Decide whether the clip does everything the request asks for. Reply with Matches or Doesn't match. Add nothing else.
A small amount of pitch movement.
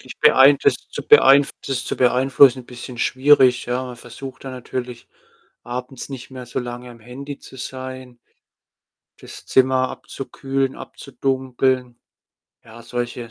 Matches